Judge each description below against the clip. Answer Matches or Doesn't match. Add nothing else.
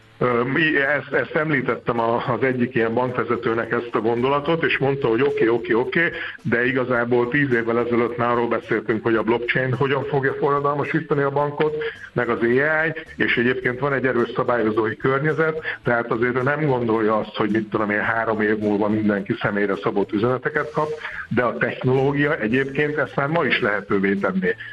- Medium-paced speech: Doesn't match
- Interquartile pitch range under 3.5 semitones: Doesn't match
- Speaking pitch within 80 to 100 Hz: Doesn't match